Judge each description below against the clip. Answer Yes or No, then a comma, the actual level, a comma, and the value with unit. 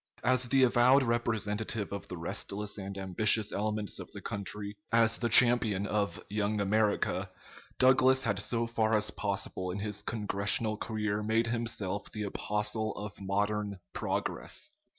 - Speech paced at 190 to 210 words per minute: No, average, 145 wpm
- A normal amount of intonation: No, narrow, 2.2 semitones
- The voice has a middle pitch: No, low, 105 Hz